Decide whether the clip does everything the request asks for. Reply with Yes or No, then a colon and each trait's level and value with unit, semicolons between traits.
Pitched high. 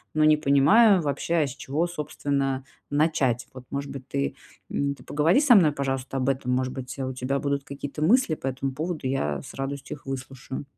No: medium, 140 Hz